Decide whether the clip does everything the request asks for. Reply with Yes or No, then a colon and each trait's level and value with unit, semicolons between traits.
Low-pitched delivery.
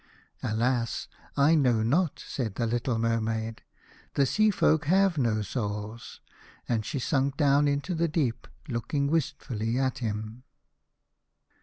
Yes: low, 125 Hz